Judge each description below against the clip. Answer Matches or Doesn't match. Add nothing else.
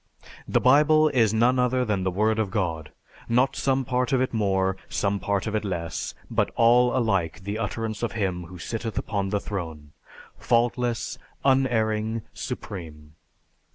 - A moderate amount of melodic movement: Matches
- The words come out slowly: Doesn't match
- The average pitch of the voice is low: Matches